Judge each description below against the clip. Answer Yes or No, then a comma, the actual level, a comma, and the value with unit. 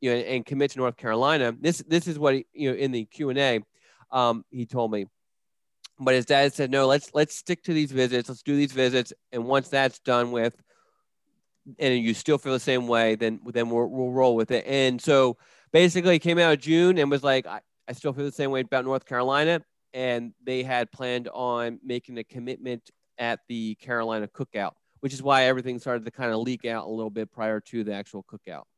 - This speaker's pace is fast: Yes, fast, 225 wpm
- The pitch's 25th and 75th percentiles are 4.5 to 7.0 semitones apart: No, average, 2.7 semitones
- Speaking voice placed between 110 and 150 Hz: Yes, low, 130 Hz